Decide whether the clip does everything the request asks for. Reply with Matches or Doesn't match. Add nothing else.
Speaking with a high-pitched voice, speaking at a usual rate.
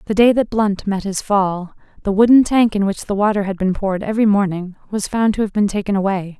Doesn't match